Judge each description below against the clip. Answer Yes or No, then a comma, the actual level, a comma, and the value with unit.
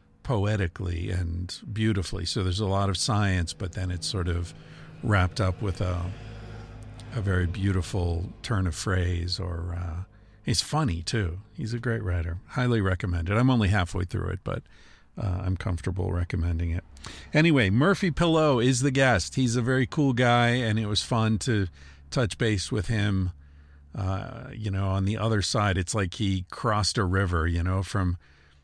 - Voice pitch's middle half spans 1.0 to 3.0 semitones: No, average, 3.9 semitones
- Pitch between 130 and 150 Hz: No, low, 100 Hz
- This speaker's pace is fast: No, average, 170 wpm